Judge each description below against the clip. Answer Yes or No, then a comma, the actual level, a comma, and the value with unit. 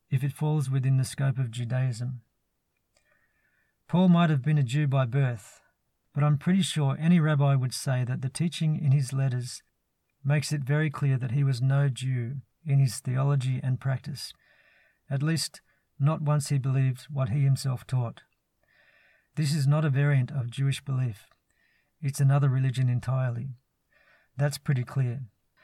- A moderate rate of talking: Yes, average, 160 wpm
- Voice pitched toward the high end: No, low, 135 Hz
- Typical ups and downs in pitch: No, narrow, 2.1 semitones